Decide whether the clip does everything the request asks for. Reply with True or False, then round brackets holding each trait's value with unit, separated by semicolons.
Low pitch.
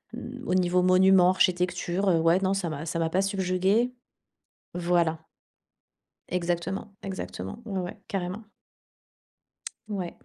False (180 Hz)